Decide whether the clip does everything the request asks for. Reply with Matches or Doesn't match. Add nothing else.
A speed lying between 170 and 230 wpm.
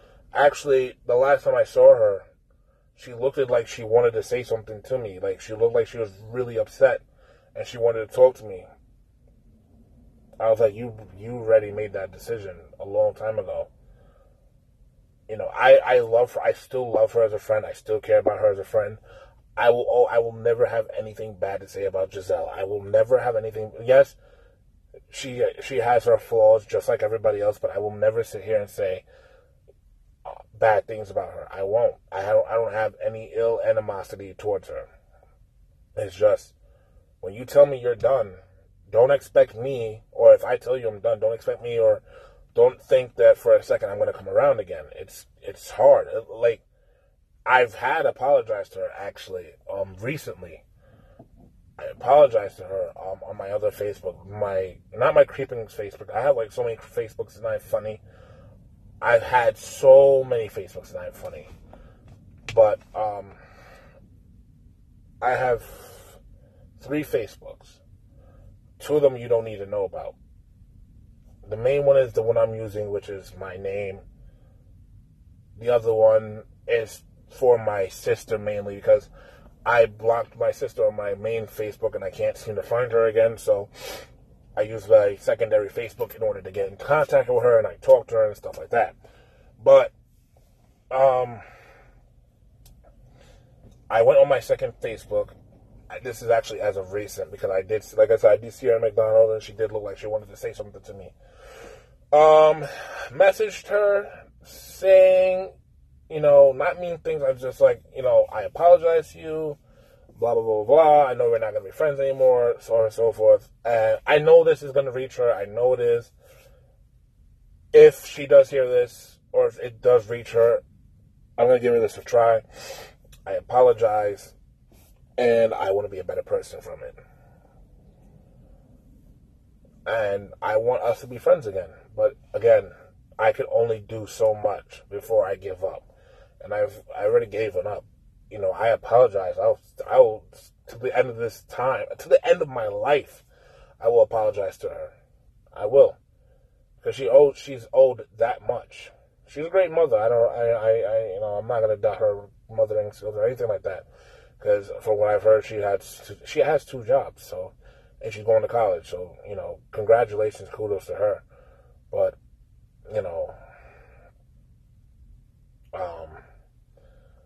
Matches